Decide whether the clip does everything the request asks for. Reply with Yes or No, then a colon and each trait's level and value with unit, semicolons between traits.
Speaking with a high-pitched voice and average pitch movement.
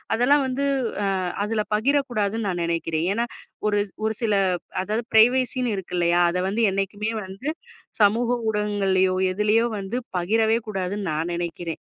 Yes: high, 210 Hz; average, 3.5 semitones